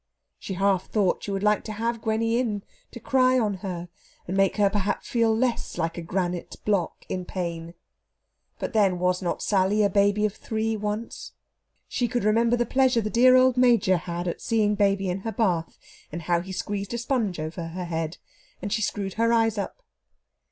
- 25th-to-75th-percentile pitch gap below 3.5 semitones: No, average, 3.9 semitones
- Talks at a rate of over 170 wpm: Yes, average, 195 wpm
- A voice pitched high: Yes, high, 205 Hz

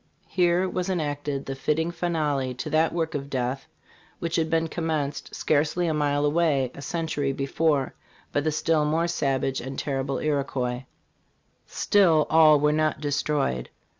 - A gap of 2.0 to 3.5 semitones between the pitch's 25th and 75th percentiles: Yes, average, 2.8 semitones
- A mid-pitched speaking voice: Yes, medium, 150 Hz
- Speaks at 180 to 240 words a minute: No, average, 155 wpm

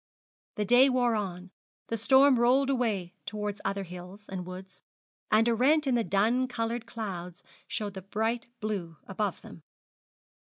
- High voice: Yes, high, 215 Hz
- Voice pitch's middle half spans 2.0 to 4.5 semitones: Yes, average, 4.1 semitones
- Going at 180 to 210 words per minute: No, average, 155 wpm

